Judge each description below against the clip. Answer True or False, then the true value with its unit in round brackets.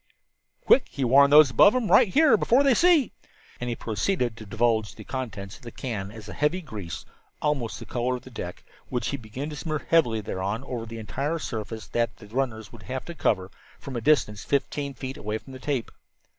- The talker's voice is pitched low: True (125 Hz)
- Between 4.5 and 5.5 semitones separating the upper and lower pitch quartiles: True (4.9 semitones)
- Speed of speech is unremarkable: False (210 wpm)